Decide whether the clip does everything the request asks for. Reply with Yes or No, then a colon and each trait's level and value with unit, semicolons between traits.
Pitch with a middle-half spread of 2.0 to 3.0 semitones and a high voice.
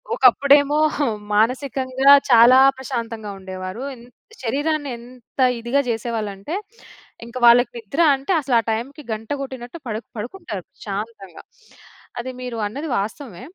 No: average, 3.6 semitones; high, 240 Hz